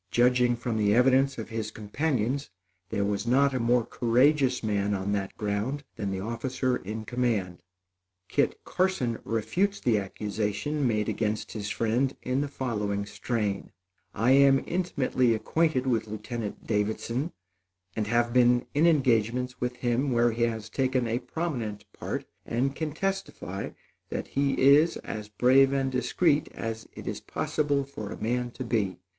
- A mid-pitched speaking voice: No, low, 120 Hz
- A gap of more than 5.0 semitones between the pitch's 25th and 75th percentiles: No, average, 3.9 semitones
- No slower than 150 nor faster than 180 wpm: Yes, average, 155 wpm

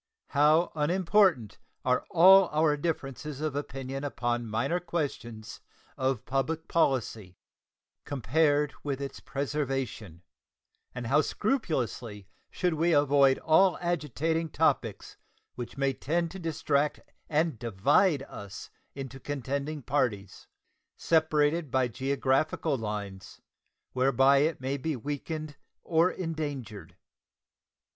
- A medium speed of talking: No, slow, 105 wpm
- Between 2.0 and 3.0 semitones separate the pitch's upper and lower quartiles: No, average, 4.0 semitones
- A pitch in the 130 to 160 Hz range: Yes, medium, 140 Hz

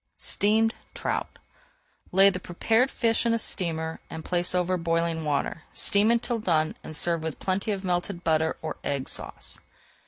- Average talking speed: Yes, average, 160 wpm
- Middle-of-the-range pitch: Yes, medium, 180 Hz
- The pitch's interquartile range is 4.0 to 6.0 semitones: Yes, average, 4.3 semitones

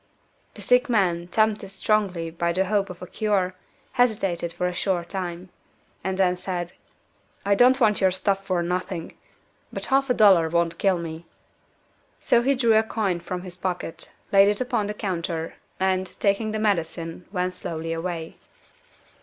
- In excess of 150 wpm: Yes, average, 165 wpm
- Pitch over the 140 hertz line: Yes, medium, 185 Hz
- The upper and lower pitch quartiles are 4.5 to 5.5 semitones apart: No, average, 3.3 semitones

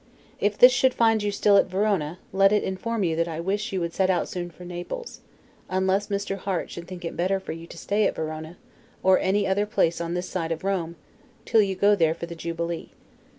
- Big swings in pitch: No, average, 3.2 semitones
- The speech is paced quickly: Yes, fast, 225 wpm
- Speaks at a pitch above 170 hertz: Yes, medium, 185 Hz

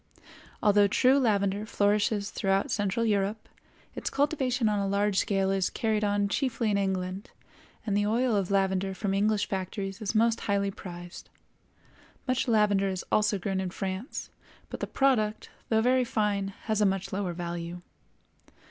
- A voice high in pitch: Yes, high, 205 Hz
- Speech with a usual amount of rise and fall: No, narrow, 2.0 semitones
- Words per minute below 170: Yes, average, 155 wpm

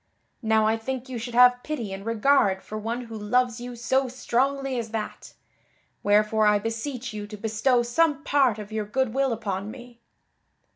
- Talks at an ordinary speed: Yes, average, 180 wpm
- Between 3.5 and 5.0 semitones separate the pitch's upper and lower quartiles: No, average, 3.0 semitones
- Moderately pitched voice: No, high, 235 Hz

